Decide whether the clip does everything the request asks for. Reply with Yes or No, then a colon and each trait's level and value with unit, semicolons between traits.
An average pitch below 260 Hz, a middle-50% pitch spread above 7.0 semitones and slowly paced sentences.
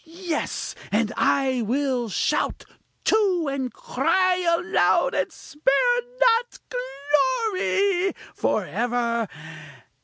No: very high, 330 Hz; wide, 7.4 semitones; slow, 90 wpm